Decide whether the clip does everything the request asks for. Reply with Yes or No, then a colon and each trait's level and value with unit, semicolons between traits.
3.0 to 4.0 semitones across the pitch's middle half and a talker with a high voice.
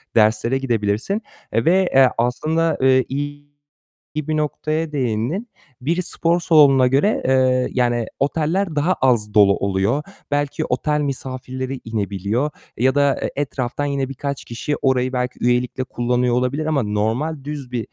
No: average, 3.5 semitones; low, 130 Hz